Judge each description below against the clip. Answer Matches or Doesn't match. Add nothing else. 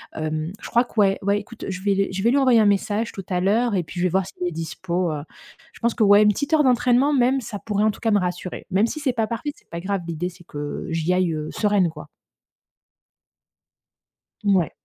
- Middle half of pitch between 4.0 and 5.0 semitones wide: Matches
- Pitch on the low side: Doesn't match